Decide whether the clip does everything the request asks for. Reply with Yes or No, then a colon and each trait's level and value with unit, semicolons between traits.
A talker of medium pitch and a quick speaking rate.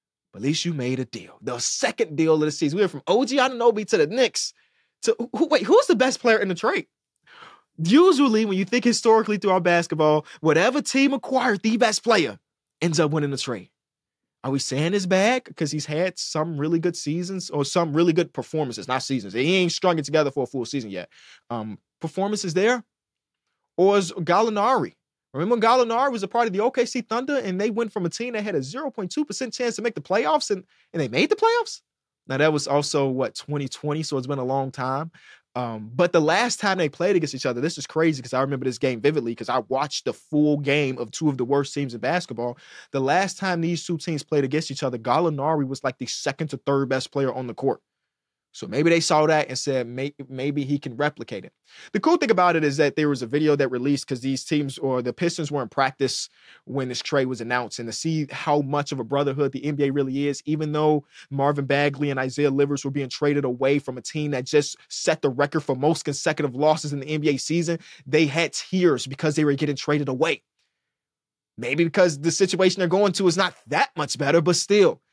Yes: medium, 155 Hz; fast, 225 wpm